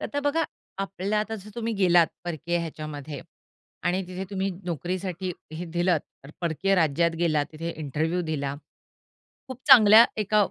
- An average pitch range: Yes, average, 3.7 semitones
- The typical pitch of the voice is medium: Yes, medium, 175 Hz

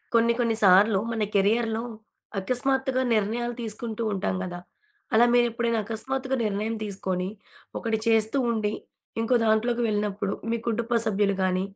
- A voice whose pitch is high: Yes, high, 220 Hz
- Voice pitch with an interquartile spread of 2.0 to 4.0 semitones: Yes, narrow, 2.4 semitones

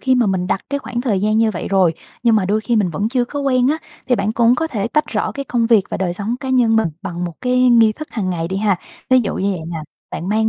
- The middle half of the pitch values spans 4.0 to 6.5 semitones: Yes, average, 4.5 semitones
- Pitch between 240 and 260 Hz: No, high, 220 Hz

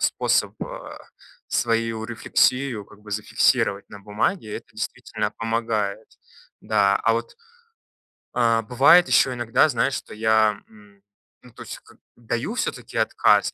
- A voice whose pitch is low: Yes, low, 115 Hz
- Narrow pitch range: Yes, narrow, 2.3 semitones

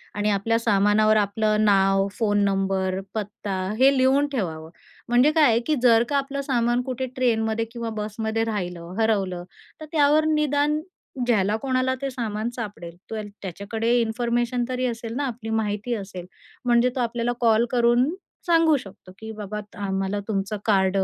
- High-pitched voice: Yes, high, 225 Hz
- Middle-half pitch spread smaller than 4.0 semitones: Yes, average, 3.6 semitones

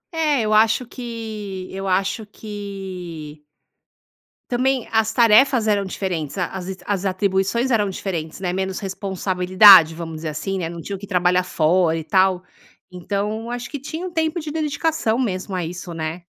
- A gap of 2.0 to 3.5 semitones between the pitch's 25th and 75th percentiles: No, average, 3.9 semitones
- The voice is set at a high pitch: Yes, high, 195 Hz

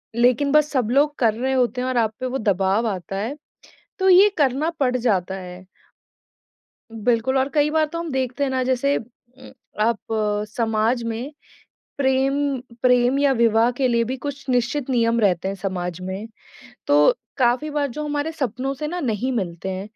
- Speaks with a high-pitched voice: Yes, very high, 250 Hz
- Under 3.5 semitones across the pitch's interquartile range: No, average, 3.8 semitones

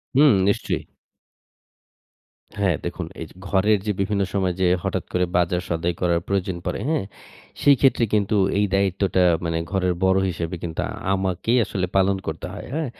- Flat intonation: Yes, narrow, 2.3 semitones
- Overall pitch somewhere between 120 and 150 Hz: No, very low, 95 Hz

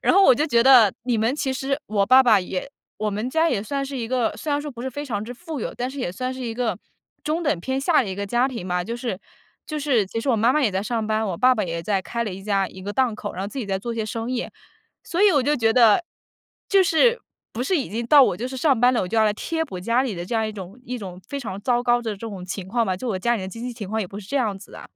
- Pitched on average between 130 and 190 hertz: No, high, 235 Hz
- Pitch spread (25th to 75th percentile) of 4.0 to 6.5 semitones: Yes, average, 4.4 semitones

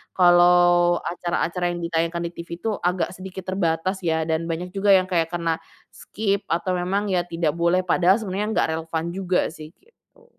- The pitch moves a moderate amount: No, narrow, 2.0 semitones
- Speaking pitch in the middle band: Yes, medium, 175 Hz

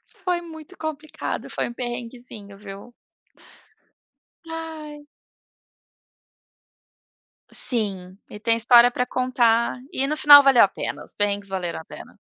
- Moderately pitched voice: No, high, 245 Hz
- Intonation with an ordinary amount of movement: No, wide, 6.3 semitones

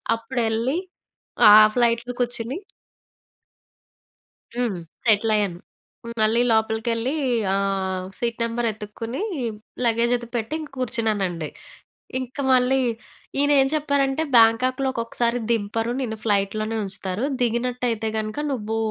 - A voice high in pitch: Yes, high, 230 Hz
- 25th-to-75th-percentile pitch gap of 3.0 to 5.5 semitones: No, narrow, 2.4 semitones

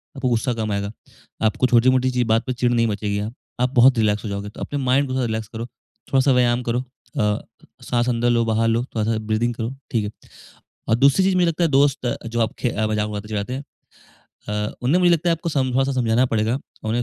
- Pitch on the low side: Yes, low, 120 Hz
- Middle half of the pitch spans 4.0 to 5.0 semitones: No, average, 2.7 semitones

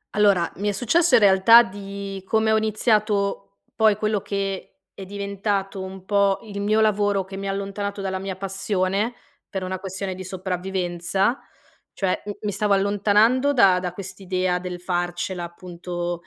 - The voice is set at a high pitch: Yes, high, 195 Hz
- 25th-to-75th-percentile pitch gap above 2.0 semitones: No, narrow, 1.7 semitones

